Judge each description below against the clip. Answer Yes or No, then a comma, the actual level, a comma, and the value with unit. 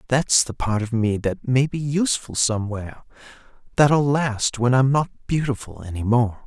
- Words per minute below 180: Yes, average, 165 wpm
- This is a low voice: Yes, low, 125 Hz